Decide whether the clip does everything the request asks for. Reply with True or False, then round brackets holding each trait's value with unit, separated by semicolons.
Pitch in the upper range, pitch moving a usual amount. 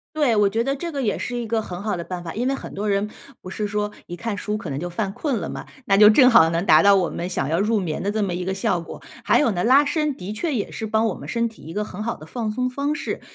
True (210 Hz; 4.3 semitones)